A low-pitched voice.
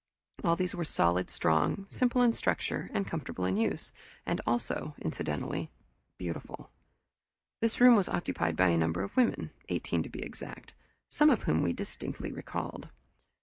No: medium, 150 Hz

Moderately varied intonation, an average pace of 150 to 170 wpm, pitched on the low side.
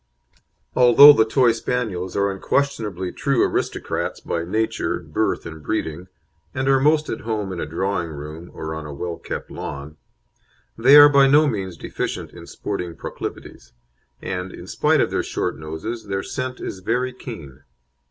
No: wide, 7.0 semitones; average, 160 wpm; low, 100 Hz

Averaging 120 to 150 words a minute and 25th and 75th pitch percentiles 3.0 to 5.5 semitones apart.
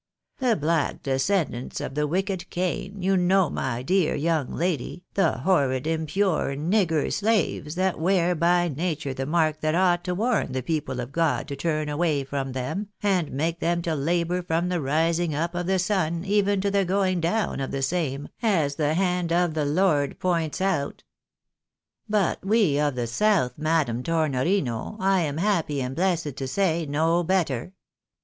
No: average, 175 wpm; average, 4.3 semitones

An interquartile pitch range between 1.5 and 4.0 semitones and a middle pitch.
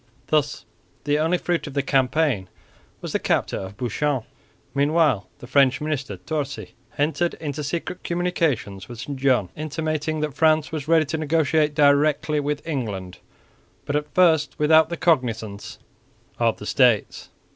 Yes: average, 3.7 semitones; medium, 145 Hz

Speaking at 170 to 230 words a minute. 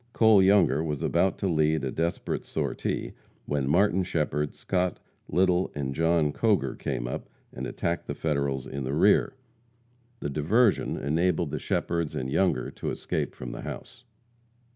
No: average, 155 wpm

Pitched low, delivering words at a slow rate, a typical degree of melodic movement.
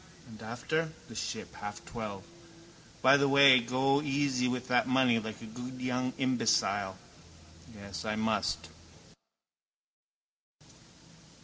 Yes: low, 125 Hz; slow, 115 wpm; average, 3.3 semitones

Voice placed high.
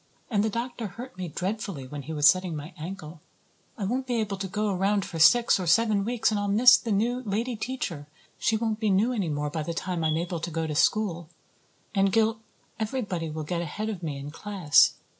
Yes: high, 195 Hz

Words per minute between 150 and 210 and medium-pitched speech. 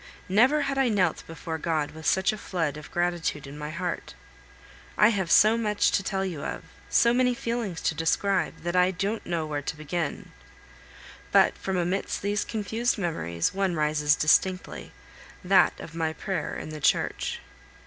Yes: average, 170 wpm; medium, 180 Hz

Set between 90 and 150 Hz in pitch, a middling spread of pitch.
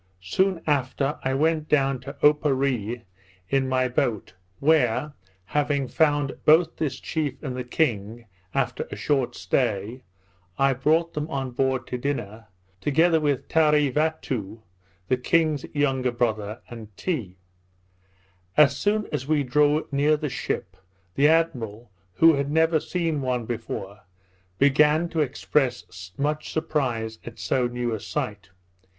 Yes: low, 135 Hz; average, 3.9 semitones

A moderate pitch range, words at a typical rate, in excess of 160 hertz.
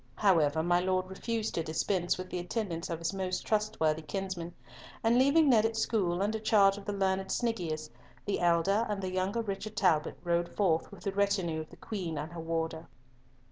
Yes: average, 3.7 semitones; average, 190 wpm; medium, 185 Hz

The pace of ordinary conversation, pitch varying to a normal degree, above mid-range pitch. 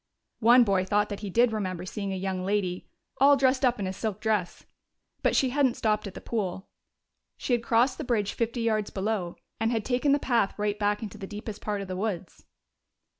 No: fast, 215 wpm; average, 3.3 semitones; high, 210 Hz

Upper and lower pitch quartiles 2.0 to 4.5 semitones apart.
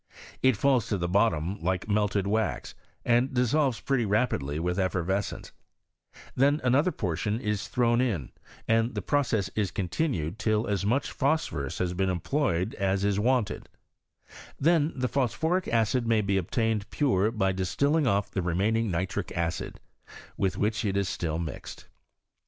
No: average, 4.9 semitones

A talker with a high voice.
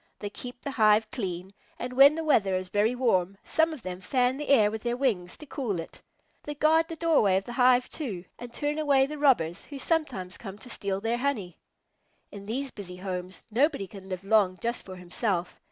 Yes: high, 225 Hz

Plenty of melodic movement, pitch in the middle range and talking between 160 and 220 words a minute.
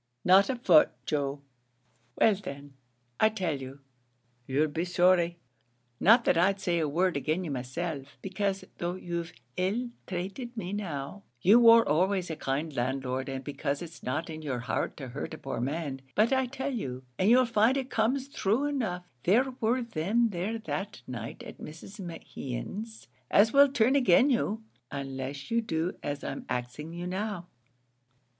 Yes: wide, 7.5 semitones; medium, 180 Hz; average, 165 wpm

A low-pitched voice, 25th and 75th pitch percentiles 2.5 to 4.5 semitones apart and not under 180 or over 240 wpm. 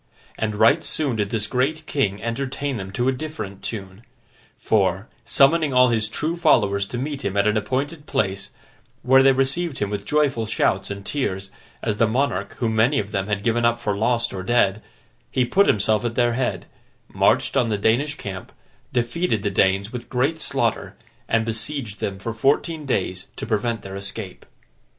No: low, 115 Hz; average, 4.9 semitones; average, 185 wpm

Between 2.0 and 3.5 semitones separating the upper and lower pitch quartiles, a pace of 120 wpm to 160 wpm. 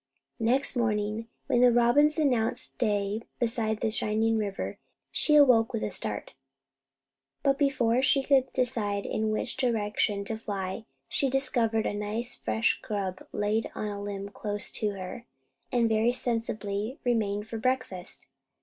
Yes: average, 3.1 semitones; average, 145 wpm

